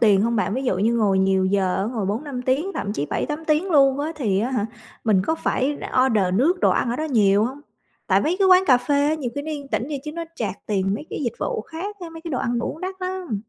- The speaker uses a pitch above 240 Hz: Yes, very high, 255 Hz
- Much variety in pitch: Yes, wide, 6.7 semitones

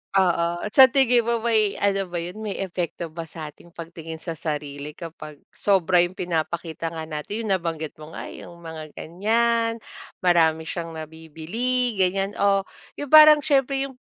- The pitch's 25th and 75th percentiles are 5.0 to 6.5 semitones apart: Yes, wide, 5.5 semitones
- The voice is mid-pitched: Yes, medium, 175 Hz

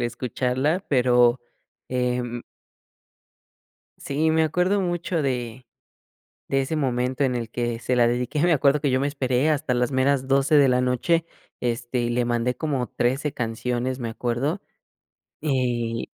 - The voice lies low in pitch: Yes, low, 125 Hz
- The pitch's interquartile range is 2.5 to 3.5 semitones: Yes, average, 2.8 semitones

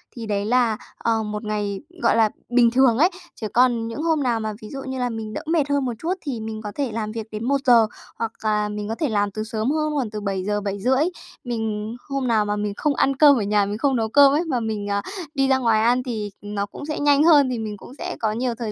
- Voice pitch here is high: Yes, high, 230 Hz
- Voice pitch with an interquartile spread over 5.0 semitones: No, average, 4.0 semitones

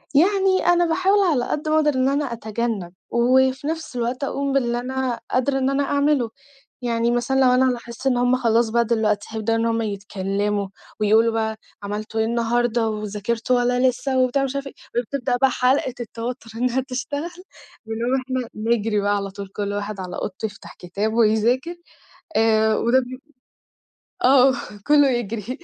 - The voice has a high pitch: Yes, high, 240 Hz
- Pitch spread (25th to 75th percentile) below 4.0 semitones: Yes, average, 3.1 semitones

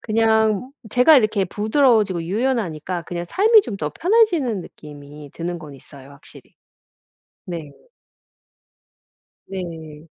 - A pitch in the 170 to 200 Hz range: Yes, high, 190 Hz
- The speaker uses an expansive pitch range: Yes, wide, 6.8 semitones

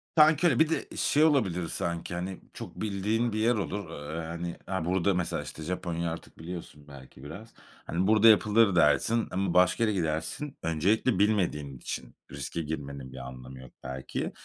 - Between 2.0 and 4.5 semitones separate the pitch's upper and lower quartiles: No, wide, 5.4 semitones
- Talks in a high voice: No, very low, 90 Hz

